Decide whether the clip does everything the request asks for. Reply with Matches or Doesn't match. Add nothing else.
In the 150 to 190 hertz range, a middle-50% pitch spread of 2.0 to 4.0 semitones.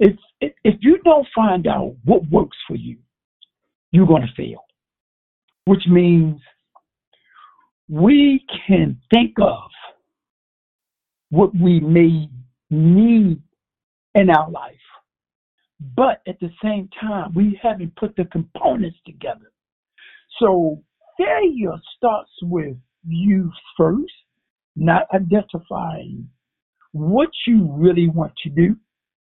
Doesn't match